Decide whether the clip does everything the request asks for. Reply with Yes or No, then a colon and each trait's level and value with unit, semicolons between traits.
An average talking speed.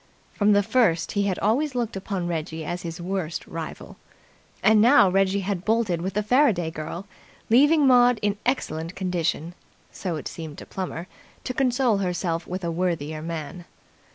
Yes: average, 165 wpm